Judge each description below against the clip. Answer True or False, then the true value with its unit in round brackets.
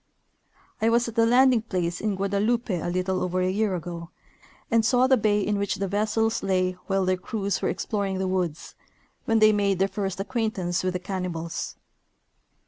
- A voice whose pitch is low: False (195 Hz)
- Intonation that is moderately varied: True (3.0 semitones)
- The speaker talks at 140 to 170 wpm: False (190 wpm)